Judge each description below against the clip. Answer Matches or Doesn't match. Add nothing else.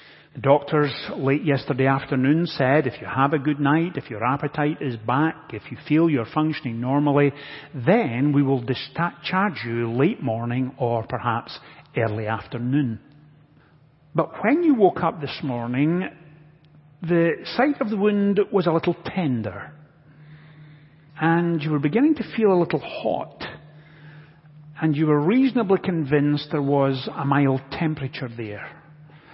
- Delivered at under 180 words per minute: Matches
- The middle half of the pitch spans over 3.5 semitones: Doesn't match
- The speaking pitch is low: Doesn't match